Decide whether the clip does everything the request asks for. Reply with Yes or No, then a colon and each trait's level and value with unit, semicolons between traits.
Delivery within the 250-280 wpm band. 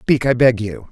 Yes: fast, 260 wpm